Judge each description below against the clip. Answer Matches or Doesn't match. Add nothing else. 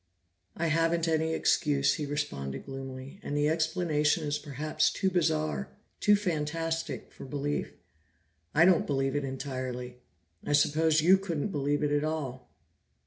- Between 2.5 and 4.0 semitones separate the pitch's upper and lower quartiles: Matches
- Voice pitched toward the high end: Doesn't match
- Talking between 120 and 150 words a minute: Matches